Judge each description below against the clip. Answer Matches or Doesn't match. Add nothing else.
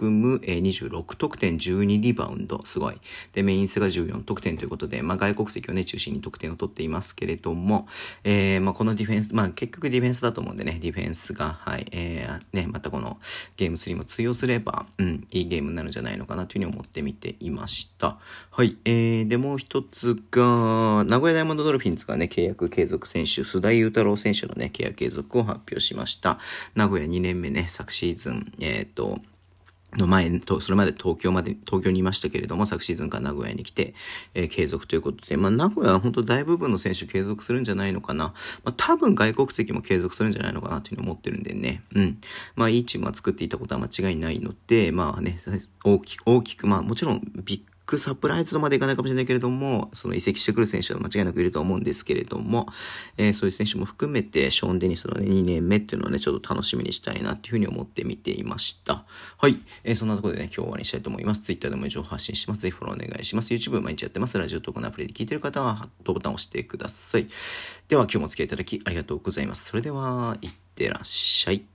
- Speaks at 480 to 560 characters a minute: Matches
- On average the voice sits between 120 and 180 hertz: Doesn't match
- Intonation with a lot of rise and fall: Doesn't match